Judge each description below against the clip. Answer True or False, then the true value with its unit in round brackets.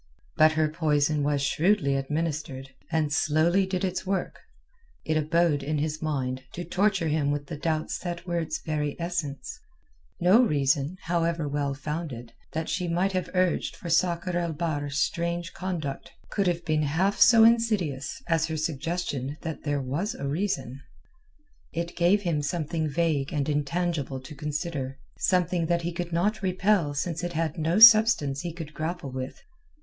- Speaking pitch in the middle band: True (160 Hz)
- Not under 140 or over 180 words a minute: True (165 wpm)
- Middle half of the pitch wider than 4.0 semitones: False (3.3 semitones)